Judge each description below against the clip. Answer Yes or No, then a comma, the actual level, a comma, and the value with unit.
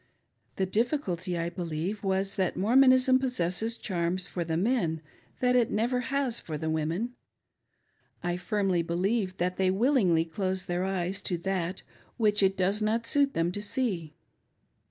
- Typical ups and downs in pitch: Yes, average, 4.7 semitones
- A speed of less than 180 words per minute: Yes, average, 155 wpm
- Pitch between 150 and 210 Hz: Yes, high, 190 Hz